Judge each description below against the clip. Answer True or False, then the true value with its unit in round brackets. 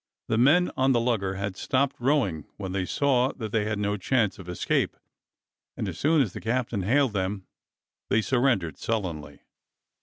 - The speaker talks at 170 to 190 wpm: True (175 wpm)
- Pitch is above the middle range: False (110 Hz)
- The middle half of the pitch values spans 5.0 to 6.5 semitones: True (5.3 semitones)